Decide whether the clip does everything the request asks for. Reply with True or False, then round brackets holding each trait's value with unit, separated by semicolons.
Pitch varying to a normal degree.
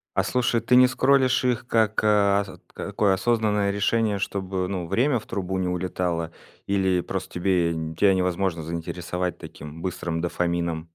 True (3.7 semitones)